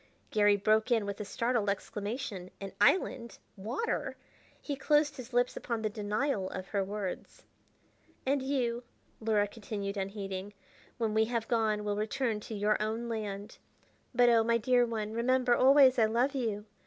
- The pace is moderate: Yes, average, 160 wpm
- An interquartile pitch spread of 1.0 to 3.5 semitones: Yes, average, 2.9 semitones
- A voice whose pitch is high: Yes, high, 220 Hz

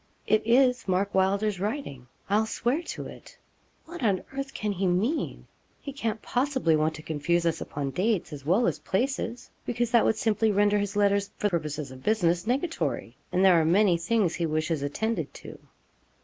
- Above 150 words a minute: Yes, average, 180 wpm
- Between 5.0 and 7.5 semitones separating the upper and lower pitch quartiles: Yes, average, 5.3 semitones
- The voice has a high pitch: Yes, high, 200 Hz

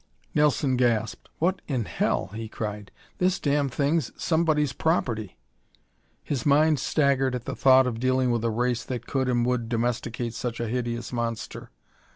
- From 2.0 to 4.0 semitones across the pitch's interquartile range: Yes, average, 3.3 semitones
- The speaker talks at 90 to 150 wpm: No, average, 160 wpm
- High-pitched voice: No, low, 125 Hz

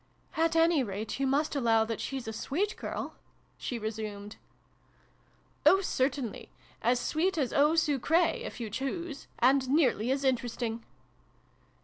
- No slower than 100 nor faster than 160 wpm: Yes, average, 150 wpm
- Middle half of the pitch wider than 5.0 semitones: Yes, wide, 5.5 semitones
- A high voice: Yes, very high, 265 Hz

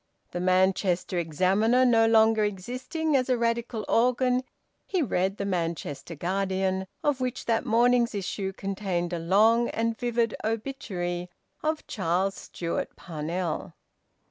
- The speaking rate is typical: No, slow, 125 wpm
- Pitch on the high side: Yes, high, 205 Hz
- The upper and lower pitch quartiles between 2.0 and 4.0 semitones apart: No, average, 4.5 semitones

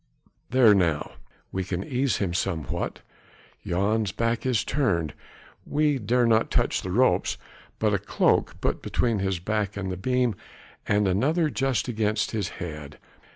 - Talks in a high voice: No, low, 105 Hz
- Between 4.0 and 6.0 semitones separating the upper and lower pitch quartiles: Yes, average, 4.8 semitones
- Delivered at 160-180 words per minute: No, average, 150 wpm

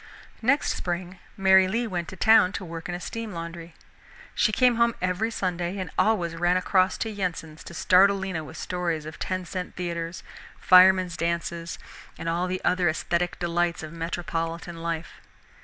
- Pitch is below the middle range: No, medium, 180 Hz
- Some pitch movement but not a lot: No, narrow, 2.1 semitones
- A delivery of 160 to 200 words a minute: Yes, average, 170 wpm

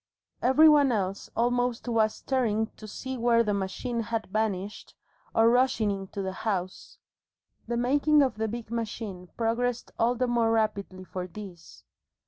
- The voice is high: Yes, high, 225 Hz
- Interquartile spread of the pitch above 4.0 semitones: No, average, 3.3 semitones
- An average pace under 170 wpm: Yes, average, 150 wpm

